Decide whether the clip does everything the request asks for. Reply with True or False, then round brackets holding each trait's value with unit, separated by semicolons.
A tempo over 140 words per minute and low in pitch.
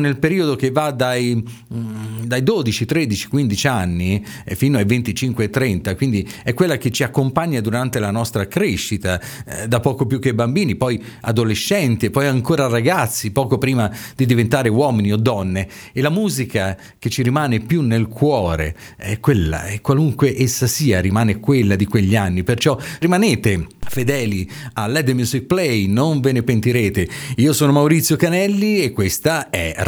True (165 wpm; 120 Hz)